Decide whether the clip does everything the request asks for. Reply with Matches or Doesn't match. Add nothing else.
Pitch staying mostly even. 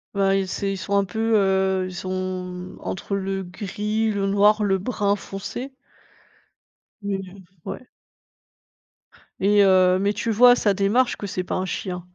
Matches